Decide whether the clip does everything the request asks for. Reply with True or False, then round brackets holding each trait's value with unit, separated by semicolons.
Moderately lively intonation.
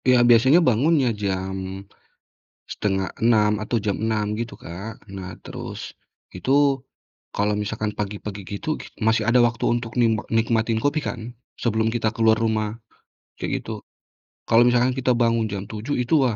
False (2.3 semitones)